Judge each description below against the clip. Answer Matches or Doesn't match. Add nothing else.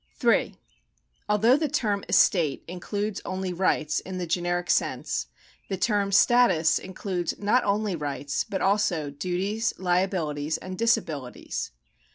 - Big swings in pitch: Doesn't match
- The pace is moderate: Doesn't match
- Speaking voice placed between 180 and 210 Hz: Matches